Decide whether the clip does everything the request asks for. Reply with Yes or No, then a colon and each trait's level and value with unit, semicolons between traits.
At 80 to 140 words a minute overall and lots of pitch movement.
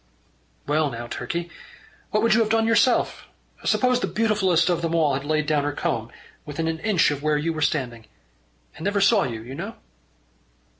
No: average, 190 wpm; wide, 6.2 semitones